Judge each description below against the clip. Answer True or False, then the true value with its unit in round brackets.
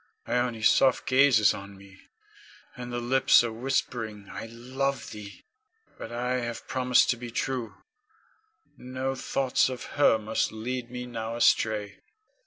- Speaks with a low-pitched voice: True (120 Hz)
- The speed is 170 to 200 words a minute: False (145 wpm)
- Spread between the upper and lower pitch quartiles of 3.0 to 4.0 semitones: False (2.5 semitones)